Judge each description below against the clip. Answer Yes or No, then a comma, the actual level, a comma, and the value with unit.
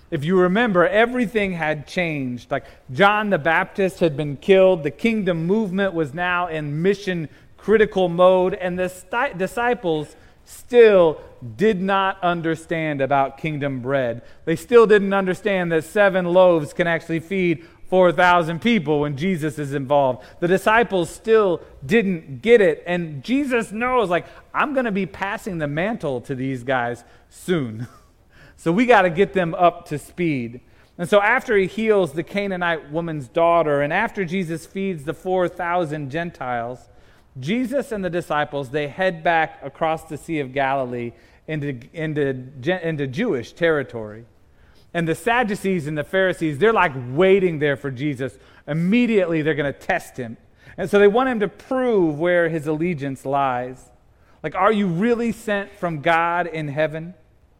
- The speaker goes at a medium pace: Yes, average, 155 wpm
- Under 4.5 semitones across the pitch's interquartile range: No, average, 4.9 semitones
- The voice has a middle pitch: Yes, medium, 170 Hz